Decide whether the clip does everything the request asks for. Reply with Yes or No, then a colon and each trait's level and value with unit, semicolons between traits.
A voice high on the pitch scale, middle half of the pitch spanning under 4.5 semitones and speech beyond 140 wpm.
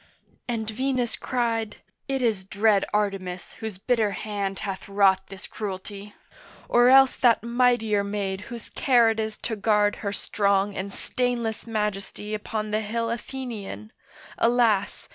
No: high, 215 Hz; average, 2.7 semitones; slow, 135 wpm